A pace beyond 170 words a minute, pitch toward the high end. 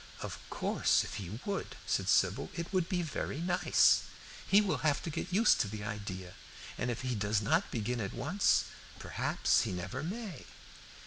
No: average, 180 wpm; low, 135 Hz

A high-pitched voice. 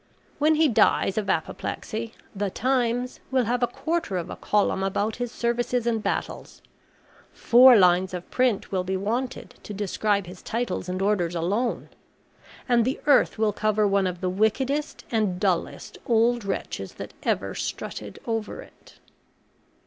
Yes: high, 220 Hz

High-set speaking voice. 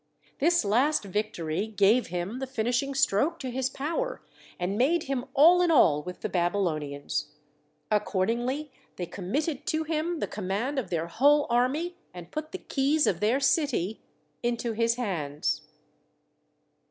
Yes: high, 240 Hz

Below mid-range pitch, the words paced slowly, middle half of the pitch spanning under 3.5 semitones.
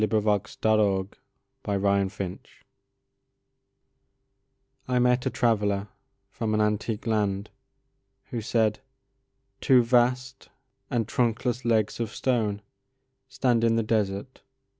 Yes: low, 110 Hz; slow, 85 wpm; average, 3.1 semitones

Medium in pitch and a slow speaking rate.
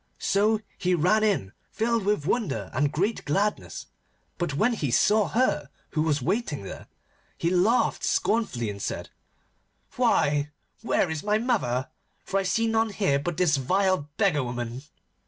No: medium, 180 Hz; average, 155 wpm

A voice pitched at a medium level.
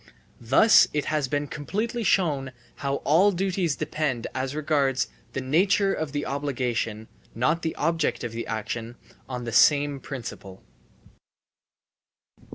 Yes: medium, 145 Hz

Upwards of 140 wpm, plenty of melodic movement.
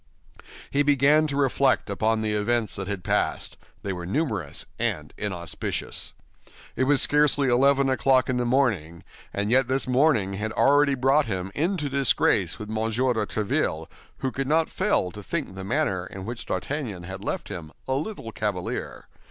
Yes: average, 170 wpm; wide, 5.8 semitones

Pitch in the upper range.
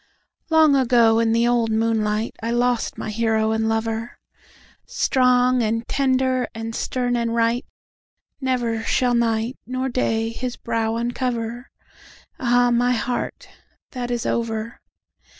Yes: high, 235 Hz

